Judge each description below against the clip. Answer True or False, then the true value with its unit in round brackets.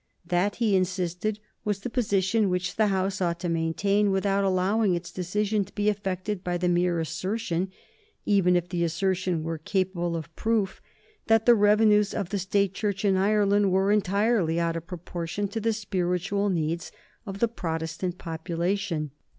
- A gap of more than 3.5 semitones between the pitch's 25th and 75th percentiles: False (2.8 semitones)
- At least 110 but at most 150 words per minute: False (165 wpm)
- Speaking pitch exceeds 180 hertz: True (190 Hz)